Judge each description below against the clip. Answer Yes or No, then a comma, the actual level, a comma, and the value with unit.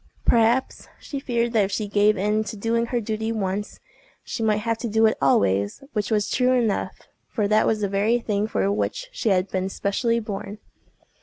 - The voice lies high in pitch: Yes, high, 215 Hz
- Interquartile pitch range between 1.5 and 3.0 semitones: Yes, narrow, 2.4 semitones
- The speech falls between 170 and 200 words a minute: Yes, average, 185 wpm